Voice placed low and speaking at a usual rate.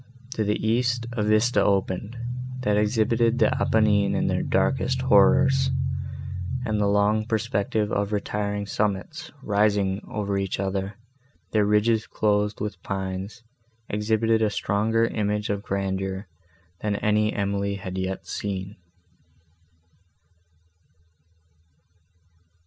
No: low, 105 Hz; slow, 115 wpm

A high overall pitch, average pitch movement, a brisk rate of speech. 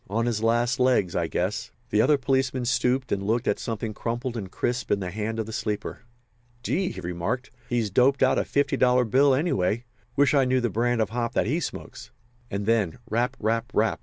No: low, 120 Hz; average, 3.0 semitones; fast, 210 wpm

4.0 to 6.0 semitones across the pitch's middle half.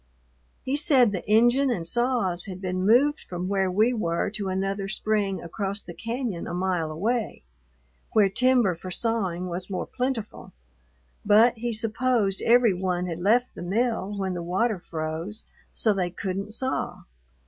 Yes: average, 4.3 semitones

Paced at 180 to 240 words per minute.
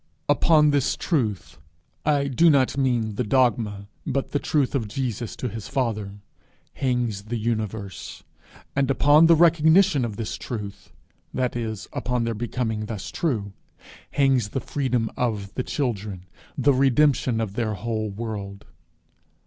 No: average, 145 wpm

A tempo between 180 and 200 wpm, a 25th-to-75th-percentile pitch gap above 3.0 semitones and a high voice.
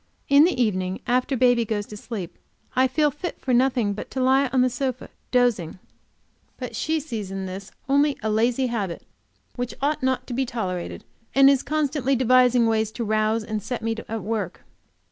Yes: average, 185 wpm; average, 3.6 semitones; high, 245 Hz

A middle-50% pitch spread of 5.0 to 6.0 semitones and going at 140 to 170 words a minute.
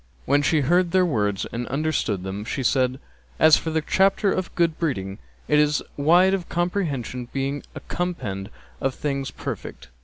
Yes: wide, 5.5 semitones; average, 165 wpm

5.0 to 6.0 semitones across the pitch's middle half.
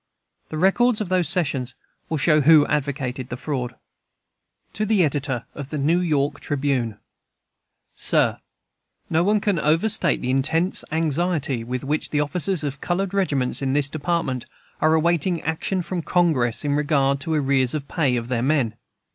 No: average, 4.0 semitones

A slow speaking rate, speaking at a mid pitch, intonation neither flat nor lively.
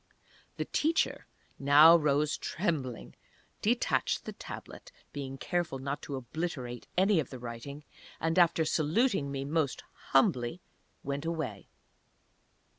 Yes: slow, 115 wpm; medium, 145 Hz; average, 3.9 semitones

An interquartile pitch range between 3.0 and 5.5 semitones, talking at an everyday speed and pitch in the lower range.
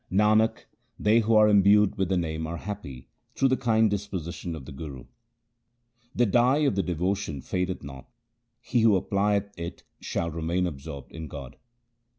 Yes: average, 4.6 semitones; average, 160 wpm; very low, 95 Hz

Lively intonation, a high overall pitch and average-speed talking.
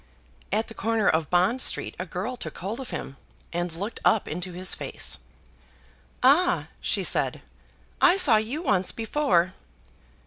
Yes: wide, 5.9 semitones; high, 210 Hz; average, 150 wpm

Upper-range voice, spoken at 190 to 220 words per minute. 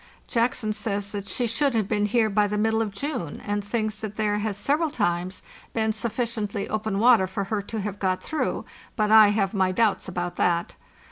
Yes: high, 210 Hz; average, 200 wpm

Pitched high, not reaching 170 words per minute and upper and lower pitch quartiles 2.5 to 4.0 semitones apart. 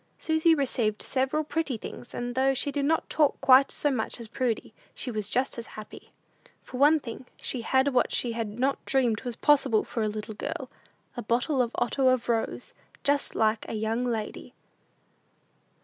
No: very high, 250 Hz; average, 180 wpm; average, 3.4 semitones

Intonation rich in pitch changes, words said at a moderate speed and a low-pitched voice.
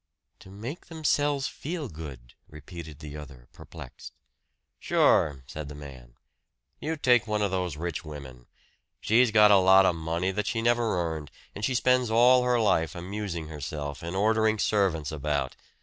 Yes: wide, 7.0 semitones; average, 160 wpm; very low, 95 Hz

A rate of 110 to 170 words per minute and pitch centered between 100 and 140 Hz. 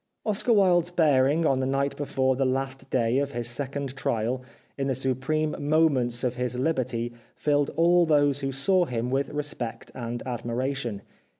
Yes: average, 165 wpm; low, 135 Hz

